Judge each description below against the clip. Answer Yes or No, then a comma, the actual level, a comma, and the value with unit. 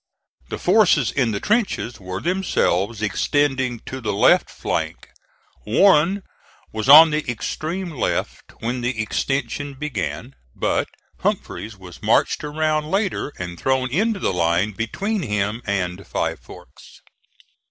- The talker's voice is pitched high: No, low, 130 Hz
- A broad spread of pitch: Yes, wide, 6.8 semitones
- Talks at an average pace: No, slow, 125 wpm